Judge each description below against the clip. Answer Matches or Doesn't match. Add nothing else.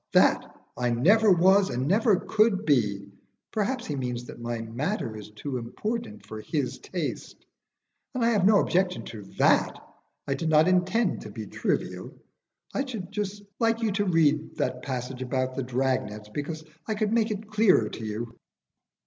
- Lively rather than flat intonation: Matches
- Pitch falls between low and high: Matches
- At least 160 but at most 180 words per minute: Matches